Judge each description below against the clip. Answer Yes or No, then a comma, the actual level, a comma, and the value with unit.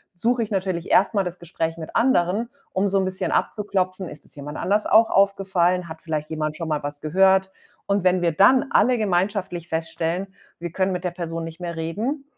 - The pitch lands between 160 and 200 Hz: Yes, medium, 185 Hz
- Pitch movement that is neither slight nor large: Yes, average, 3.2 semitones